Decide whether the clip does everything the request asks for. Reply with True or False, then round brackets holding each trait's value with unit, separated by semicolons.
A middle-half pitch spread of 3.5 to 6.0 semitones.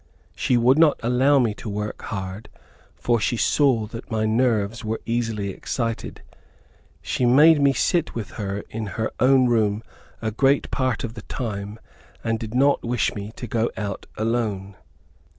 False (2.9 semitones)